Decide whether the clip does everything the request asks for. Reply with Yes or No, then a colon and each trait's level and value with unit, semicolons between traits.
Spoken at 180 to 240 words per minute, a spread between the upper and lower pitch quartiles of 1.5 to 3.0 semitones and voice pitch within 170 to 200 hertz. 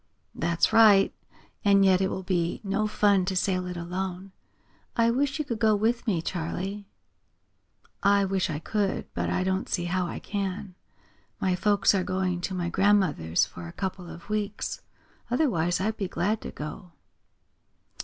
No: average, 165 wpm; narrow, 2.5 semitones; high, 190 Hz